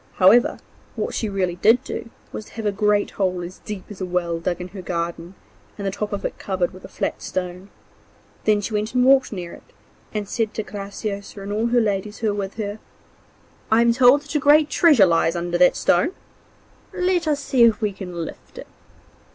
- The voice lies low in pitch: No, high, 205 Hz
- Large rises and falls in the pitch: No, average, 4.0 semitones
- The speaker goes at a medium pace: No, fast, 215 wpm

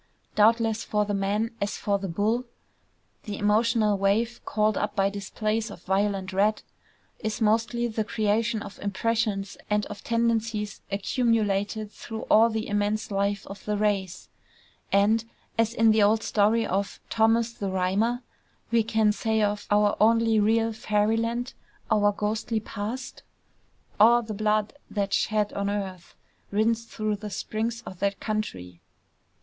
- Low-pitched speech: No, high, 215 Hz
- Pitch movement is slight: Yes, narrow, 1.8 semitones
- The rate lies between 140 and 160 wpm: Yes, average, 145 wpm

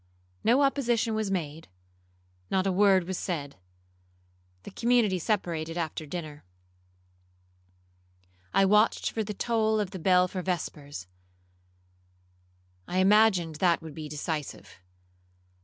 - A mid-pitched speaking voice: Yes, medium, 165 Hz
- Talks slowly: Yes, slow, 105 wpm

